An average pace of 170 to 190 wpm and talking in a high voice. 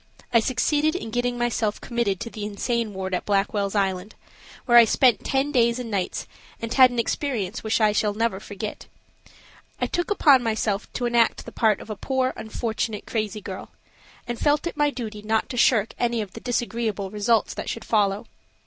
Yes: average, 185 wpm; high, 225 Hz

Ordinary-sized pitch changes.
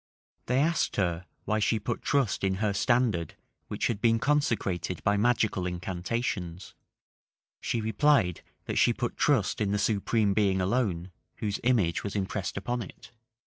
Yes: average, 3.9 semitones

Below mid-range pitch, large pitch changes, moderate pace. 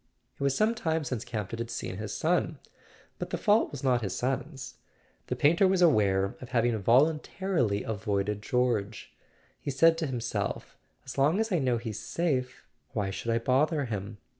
Yes: low, 125 Hz; wide, 6.5 semitones; average, 180 wpm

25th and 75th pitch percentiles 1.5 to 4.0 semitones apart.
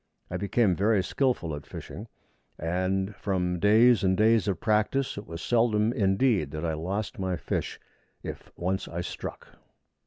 Yes: average, 3.5 semitones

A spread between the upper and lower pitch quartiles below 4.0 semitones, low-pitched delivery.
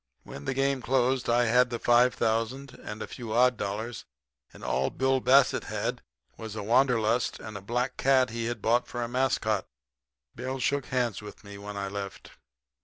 Yes: average, 2.9 semitones; low, 120 Hz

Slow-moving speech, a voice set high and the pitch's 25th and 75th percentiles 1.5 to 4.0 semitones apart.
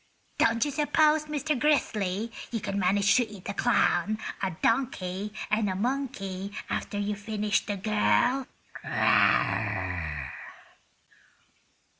No: slow, 110 wpm; high, 215 Hz; average, 4.8 semitones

